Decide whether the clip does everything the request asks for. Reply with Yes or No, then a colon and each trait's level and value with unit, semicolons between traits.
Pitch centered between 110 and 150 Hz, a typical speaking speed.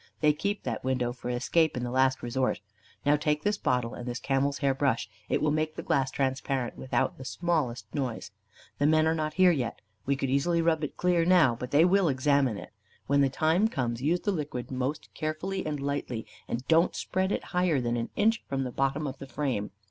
No: medium, 140 Hz; fast, 215 wpm